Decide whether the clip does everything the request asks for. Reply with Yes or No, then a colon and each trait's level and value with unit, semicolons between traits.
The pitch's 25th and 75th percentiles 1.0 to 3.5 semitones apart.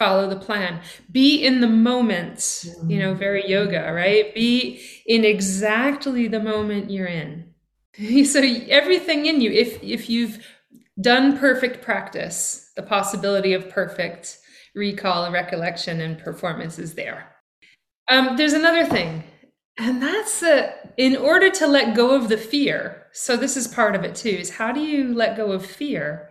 No: wide, 5.4 semitones